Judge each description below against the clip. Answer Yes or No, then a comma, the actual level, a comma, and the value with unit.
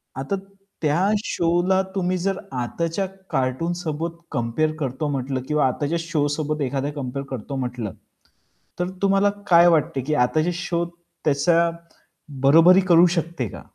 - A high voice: No, medium, 155 Hz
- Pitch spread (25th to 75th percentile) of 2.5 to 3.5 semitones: No, average, 4.0 semitones